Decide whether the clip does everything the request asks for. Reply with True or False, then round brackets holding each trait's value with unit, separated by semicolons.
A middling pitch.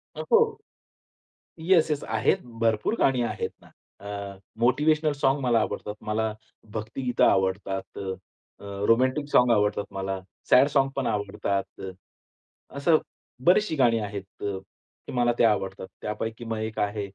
False (115 Hz)